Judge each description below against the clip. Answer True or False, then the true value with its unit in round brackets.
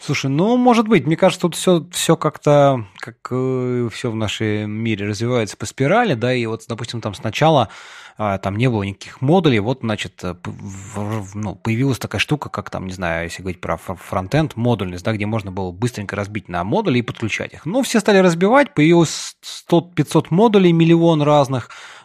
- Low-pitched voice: True (120 Hz)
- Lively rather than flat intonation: True (6.6 semitones)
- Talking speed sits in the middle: False (190 wpm)